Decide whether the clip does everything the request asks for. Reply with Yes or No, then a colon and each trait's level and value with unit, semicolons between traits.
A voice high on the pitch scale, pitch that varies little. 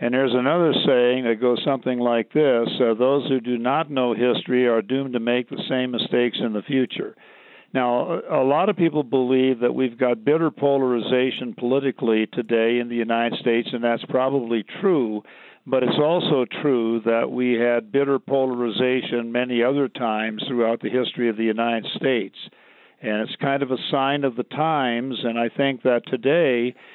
No: low, 125 Hz; narrow, 2.0 semitones